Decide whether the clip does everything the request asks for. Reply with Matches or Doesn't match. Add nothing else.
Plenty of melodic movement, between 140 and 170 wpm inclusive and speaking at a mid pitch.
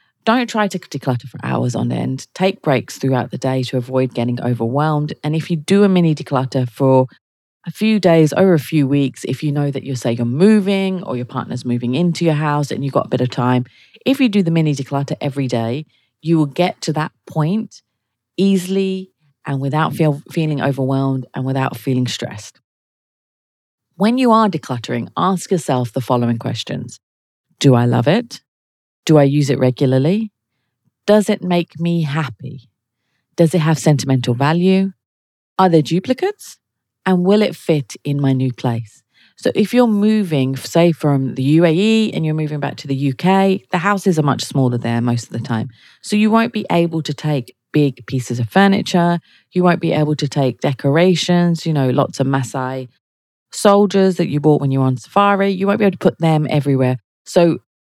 Doesn't match